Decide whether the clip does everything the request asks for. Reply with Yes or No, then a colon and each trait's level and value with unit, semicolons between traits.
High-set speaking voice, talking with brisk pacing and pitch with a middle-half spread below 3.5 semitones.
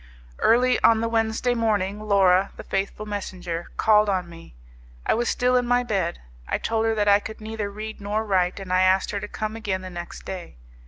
Yes: high, 205 Hz; fast, 210 wpm; average, 2.8 semitones